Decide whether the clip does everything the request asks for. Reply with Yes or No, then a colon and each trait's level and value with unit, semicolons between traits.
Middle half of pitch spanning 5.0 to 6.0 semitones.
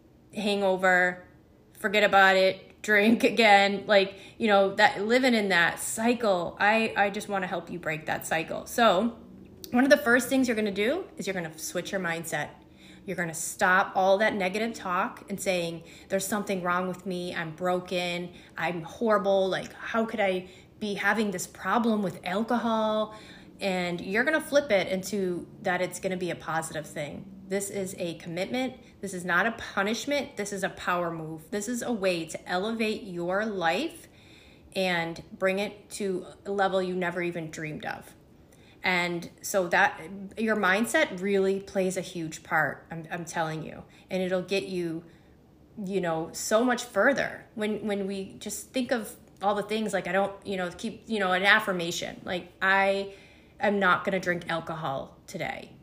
No: average, 2.9 semitones